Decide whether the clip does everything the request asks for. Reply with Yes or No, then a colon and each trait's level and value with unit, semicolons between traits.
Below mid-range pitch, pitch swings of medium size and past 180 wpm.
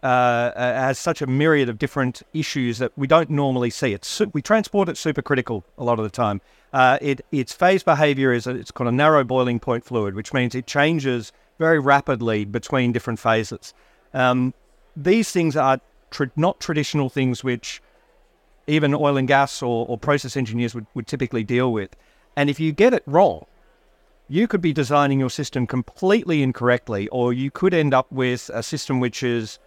Yes: low, 130 Hz; average, 3.6 semitones; average, 190 wpm